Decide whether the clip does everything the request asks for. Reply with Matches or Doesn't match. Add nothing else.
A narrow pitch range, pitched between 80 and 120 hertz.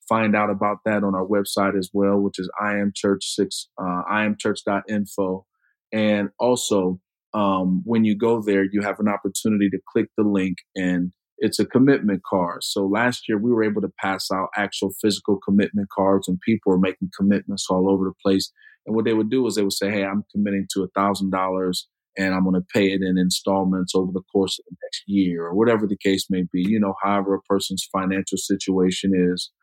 Matches